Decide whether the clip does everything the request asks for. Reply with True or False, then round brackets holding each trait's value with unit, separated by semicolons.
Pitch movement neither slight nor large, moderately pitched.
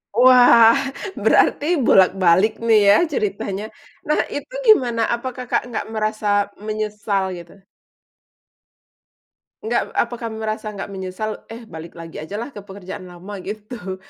False (3.3 semitones; 215 Hz)